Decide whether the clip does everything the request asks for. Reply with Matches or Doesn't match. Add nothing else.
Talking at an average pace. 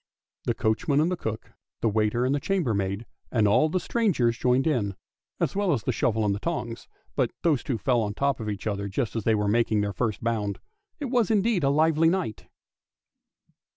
Doesn't match